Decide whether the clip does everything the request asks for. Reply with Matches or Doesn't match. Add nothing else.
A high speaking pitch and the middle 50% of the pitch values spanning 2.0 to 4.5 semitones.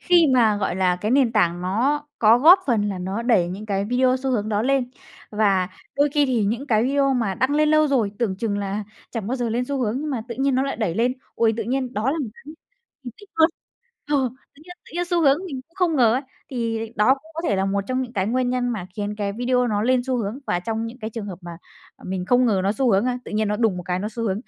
Matches